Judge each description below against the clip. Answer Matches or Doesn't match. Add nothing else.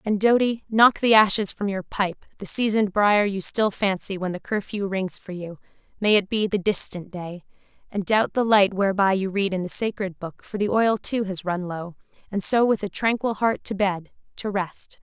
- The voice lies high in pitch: Matches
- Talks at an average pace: Doesn't match